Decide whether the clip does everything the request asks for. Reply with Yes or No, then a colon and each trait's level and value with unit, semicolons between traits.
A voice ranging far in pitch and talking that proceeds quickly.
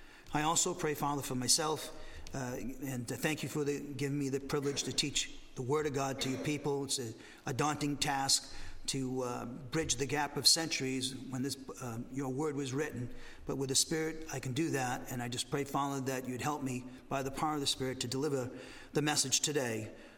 No: narrow, 2.4 semitones; fast, 215 wpm